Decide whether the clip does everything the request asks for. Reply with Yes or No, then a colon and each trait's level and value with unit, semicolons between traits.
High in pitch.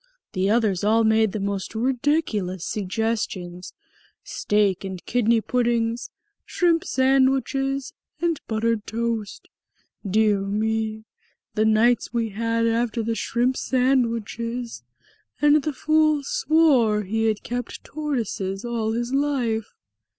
Yes: high, 230 Hz